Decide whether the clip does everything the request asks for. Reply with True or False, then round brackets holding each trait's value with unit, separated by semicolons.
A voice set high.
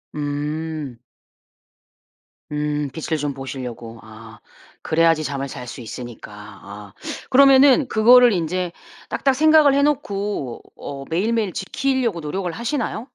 False (160 Hz)